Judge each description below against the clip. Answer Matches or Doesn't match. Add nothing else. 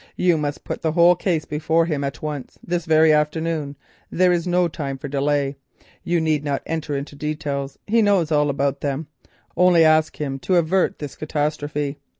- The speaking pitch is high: Doesn't match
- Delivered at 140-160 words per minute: Doesn't match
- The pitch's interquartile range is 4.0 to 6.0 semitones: Doesn't match